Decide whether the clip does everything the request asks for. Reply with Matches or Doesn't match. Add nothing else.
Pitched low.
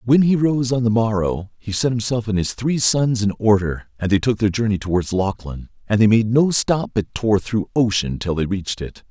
Matches